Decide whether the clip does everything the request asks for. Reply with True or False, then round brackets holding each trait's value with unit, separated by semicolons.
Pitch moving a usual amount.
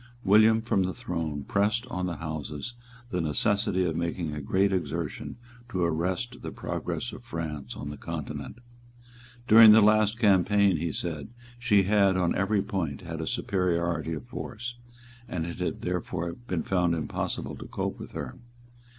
True (4.0 semitones)